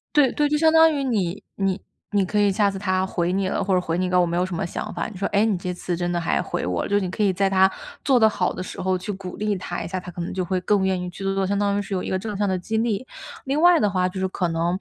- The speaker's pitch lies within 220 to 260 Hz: No, high, 190 Hz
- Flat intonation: Yes, narrow, 2.3 semitones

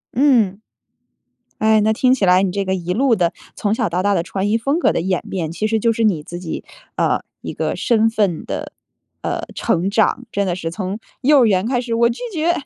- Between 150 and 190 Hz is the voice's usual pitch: No, high, 210 Hz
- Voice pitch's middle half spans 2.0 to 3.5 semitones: No, average, 4.1 semitones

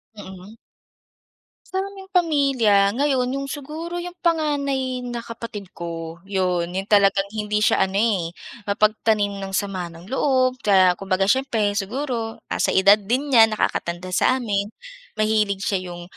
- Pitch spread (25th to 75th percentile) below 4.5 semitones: No, average, 5.2 semitones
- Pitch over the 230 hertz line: No, high, 210 Hz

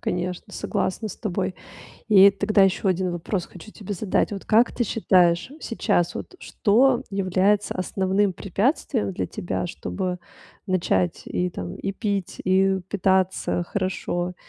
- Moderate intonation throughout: No, narrow, 2.2 semitones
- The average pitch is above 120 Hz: Yes, high, 190 Hz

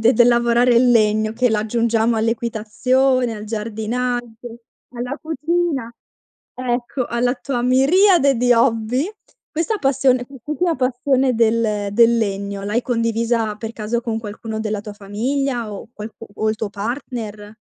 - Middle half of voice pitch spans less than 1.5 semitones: No, narrow, 2.6 semitones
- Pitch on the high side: Yes, high, 235 Hz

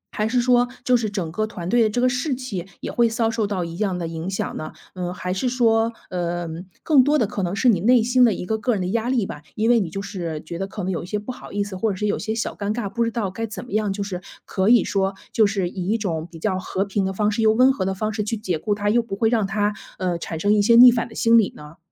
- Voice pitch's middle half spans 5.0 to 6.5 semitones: No, average, 3.6 semitones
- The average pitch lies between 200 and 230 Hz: Yes, high, 210 Hz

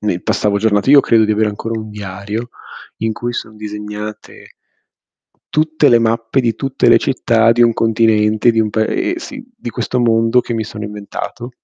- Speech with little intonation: Yes, narrow, 2.2 semitones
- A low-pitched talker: Yes, low, 115 Hz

